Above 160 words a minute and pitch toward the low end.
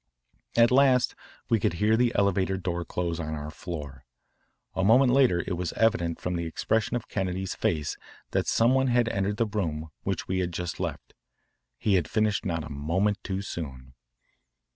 Yes: average, 180 wpm; very low, 95 Hz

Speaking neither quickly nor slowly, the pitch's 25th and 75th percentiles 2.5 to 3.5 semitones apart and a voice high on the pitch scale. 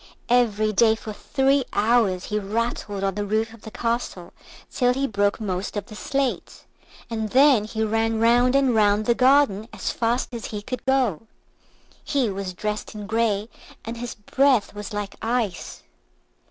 Yes: average, 165 wpm; average, 2.9 semitones; high, 220 Hz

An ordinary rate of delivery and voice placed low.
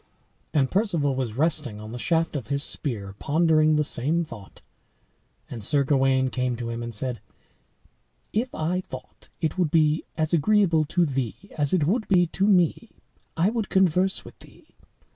No: average, 170 wpm; medium, 155 Hz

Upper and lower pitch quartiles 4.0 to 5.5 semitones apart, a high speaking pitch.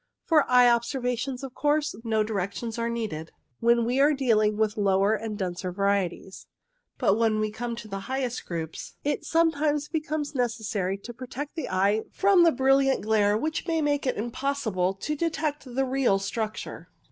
Yes: average, 5.0 semitones; high, 235 Hz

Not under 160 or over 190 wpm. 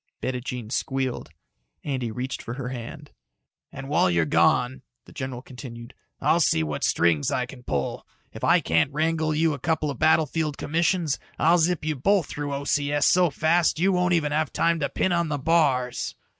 Yes: average, 180 wpm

